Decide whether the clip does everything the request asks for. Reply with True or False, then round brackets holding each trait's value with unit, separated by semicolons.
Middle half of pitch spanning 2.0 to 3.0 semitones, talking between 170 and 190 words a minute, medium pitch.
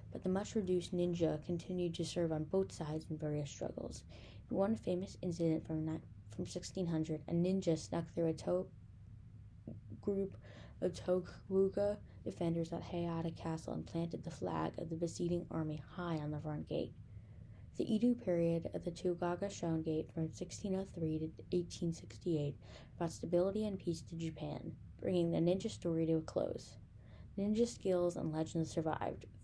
False (2.5 semitones; 155 wpm; 165 Hz)